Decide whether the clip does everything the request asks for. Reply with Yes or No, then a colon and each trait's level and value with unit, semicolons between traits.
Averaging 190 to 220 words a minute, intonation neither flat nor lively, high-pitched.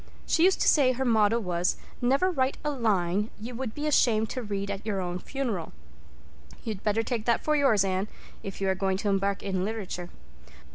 Yes: average, 200 wpm; average, 4.6 semitones; high, 215 Hz